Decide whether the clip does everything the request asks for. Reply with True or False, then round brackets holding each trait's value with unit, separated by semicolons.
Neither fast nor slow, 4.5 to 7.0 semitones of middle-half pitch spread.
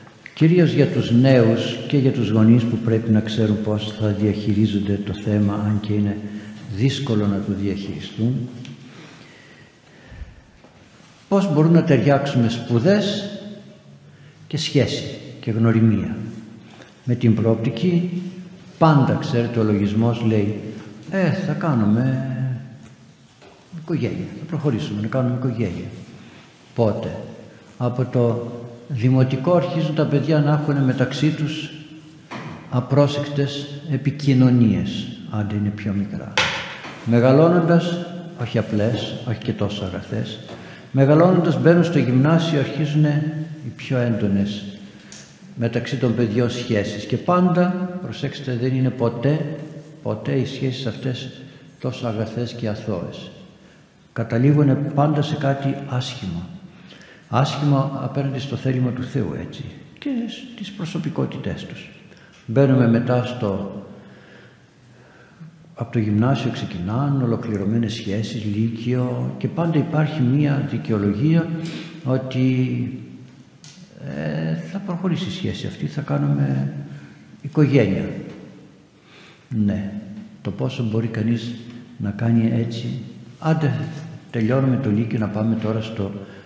False (110 wpm; 5.2 semitones)